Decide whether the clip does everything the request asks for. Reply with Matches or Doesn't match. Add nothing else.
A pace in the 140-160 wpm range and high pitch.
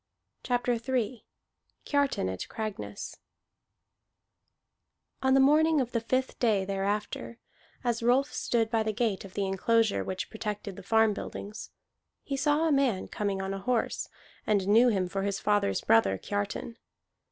Matches